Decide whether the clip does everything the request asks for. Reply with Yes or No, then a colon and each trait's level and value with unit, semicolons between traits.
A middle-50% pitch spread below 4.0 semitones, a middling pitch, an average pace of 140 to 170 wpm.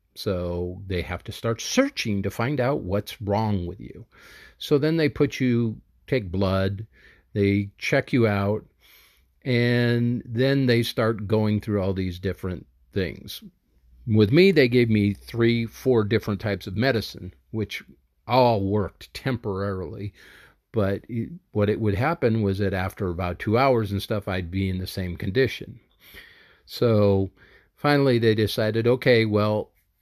No: average, 3.5 semitones; low, 105 Hz; average, 150 wpm